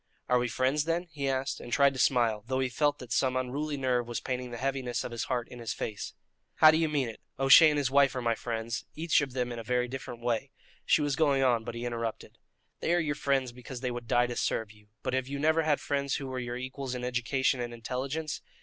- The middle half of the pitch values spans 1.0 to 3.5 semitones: Yes, narrow, 2.6 semitones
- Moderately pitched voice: No, low, 130 Hz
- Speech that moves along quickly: Yes, fast, 260 wpm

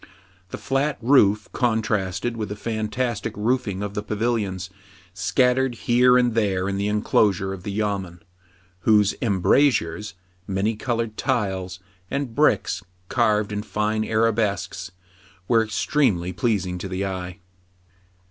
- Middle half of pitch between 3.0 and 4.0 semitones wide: Yes, average, 3.4 semitones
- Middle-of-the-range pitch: No, low, 105 Hz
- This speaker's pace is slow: Yes, slow, 125 wpm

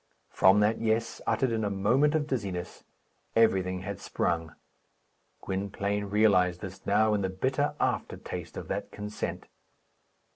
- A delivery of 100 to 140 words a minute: Yes, slow, 135 wpm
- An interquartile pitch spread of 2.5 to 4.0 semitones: Yes, average, 2.9 semitones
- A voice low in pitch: Yes, low, 105 Hz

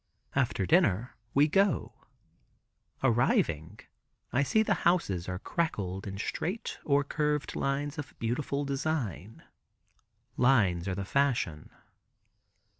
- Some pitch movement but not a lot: No, wide, 7.3 semitones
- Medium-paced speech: No, slow, 110 wpm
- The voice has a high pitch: No, low, 135 Hz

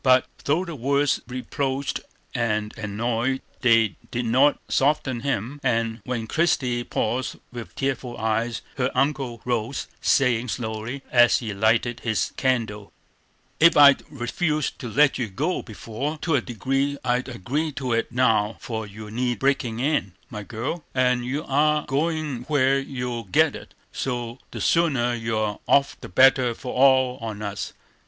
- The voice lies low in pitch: Yes, low, 125 Hz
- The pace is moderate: Yes, average, 145 wpm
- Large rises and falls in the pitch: No, average, 3.3 semitones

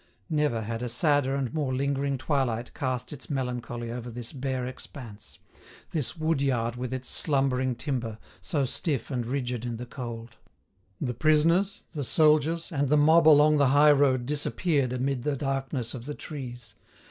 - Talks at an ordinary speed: Yes, average, 160 wpm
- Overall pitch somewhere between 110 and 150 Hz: Yes, low, 135 Hz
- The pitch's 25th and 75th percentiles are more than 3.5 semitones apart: No, average, 3.2 semitones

